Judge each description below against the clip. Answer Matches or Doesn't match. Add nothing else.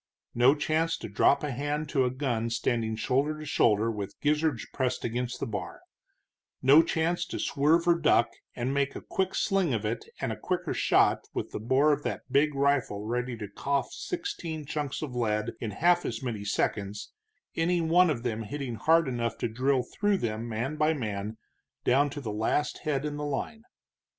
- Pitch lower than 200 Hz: Matches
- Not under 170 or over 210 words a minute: Matches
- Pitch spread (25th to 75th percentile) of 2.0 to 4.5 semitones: Doesn't match